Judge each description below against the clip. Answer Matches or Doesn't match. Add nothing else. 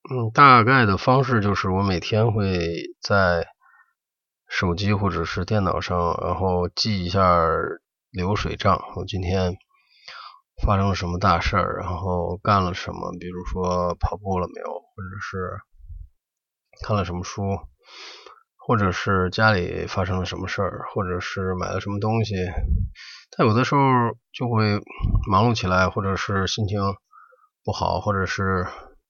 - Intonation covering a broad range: Doesn't match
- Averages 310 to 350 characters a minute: Doesn't match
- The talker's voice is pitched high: Doesn't match